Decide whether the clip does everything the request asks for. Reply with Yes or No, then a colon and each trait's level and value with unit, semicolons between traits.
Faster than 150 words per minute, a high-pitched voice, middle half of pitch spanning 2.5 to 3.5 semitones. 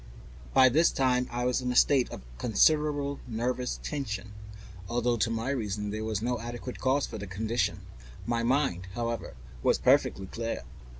No: average, 165 wpm; low, 120 Hz; average, 3.0 semitones